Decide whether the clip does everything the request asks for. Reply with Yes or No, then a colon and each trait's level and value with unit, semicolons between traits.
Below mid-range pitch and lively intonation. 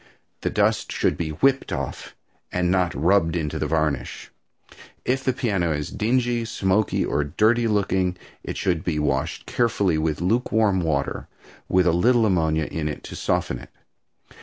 Yes: very low, 90 Hz; wide, 5.8 semitones